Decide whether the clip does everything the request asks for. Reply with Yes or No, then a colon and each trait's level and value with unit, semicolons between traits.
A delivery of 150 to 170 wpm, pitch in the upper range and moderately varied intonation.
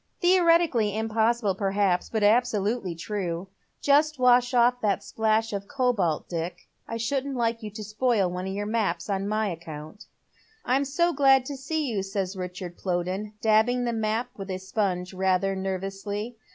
Yes: average, 165 wpm; high, 215 Hz; average, 4.3 semitones